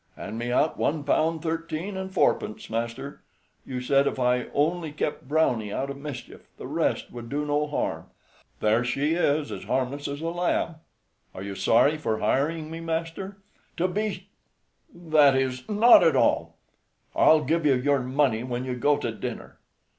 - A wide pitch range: No, average, 4.4 semitones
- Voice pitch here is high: No, medium, 145 Hz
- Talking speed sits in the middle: Yes, average, 170 wpm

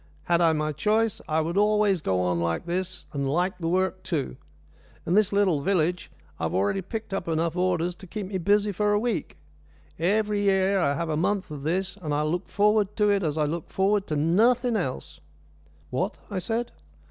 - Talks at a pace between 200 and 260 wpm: Yes, fast, 205 wpm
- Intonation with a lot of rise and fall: No, average, 4.3 semitones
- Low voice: No, medium, 185 Hz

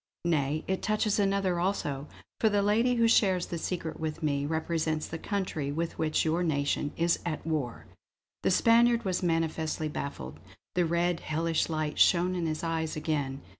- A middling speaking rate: Yes, average, 170 wpm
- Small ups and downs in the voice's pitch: No, average, 3.1 semitones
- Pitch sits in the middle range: Yes, medium, 165 Hz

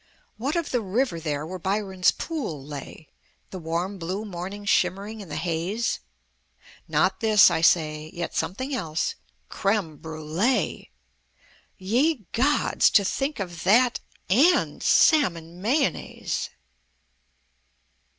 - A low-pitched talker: No, high, 190 Hz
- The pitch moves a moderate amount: No, wide, 5.8 semitones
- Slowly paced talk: Yes, slow, 115 wpm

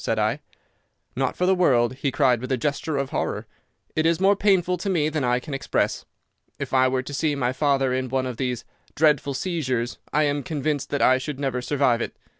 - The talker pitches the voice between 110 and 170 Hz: Yes, low, 135 Hz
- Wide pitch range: No, average, 3.2 semitones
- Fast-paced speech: Yes, fast, 220 wpm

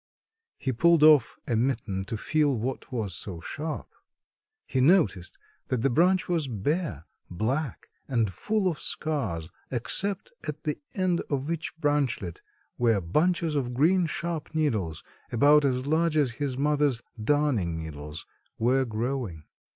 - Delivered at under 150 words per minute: Yes, average, 140 wpm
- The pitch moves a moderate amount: No, wide, 5.9 semitones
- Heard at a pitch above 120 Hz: Yes, low, 135 Hz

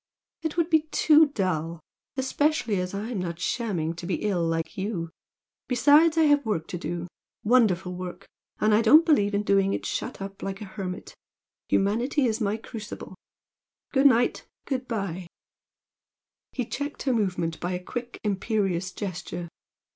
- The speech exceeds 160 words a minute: No, average, 155 wpm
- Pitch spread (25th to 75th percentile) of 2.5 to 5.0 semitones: No, wide, 5.6 semitones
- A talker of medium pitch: No, high, 205 Hz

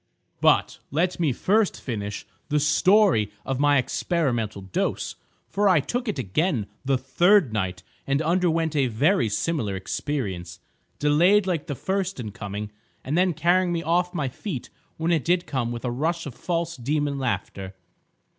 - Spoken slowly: No, average, 165 wpm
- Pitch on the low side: No, medium, 145 Hz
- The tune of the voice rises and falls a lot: Yes, wide, 6.5 semitones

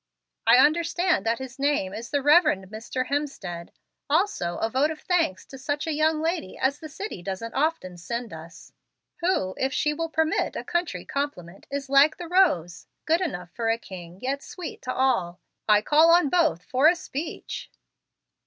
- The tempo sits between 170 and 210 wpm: Yes, average, 180 wpm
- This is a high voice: Yes, very high, 280 Hz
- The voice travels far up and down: Yes, wide, 7.2 semitones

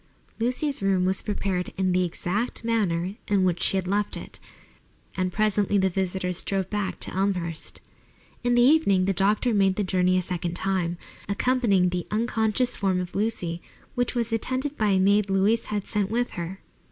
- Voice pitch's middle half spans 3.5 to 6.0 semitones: No, average, 3.1 semitones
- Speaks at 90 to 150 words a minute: No, average, 175 wpm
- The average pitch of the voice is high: Yes, high, 195 Hz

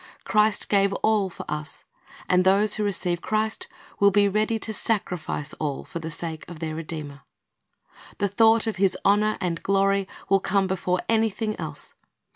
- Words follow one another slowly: No, average, 175 wpm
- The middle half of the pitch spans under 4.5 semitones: Yes, average, 3.6 semitones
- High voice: Yes, high, 195 Hz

